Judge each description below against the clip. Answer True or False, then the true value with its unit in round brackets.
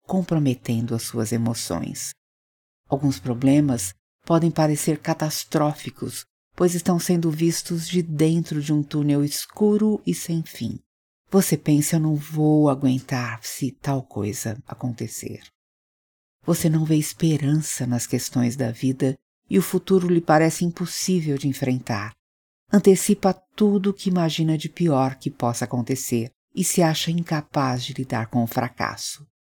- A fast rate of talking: False (135 wpm)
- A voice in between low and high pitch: True (145 Hz)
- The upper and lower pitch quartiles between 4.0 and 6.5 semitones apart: True (5.1 semitones)